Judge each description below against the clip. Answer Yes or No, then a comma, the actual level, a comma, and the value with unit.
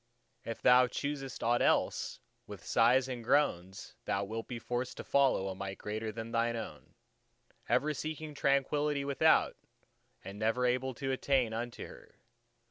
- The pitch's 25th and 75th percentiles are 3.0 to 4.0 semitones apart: Yes, average, 3.3 semitones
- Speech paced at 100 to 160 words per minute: Yes, average, 150 wpm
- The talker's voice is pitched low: Yes, low, 125 Hz